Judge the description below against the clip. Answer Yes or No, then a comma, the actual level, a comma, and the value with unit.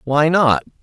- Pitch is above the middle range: No, medium, 150 Hz